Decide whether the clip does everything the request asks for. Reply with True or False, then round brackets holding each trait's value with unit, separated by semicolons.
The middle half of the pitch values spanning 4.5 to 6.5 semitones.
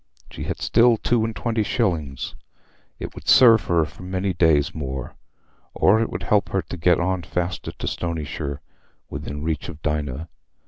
True (5.1 semitones)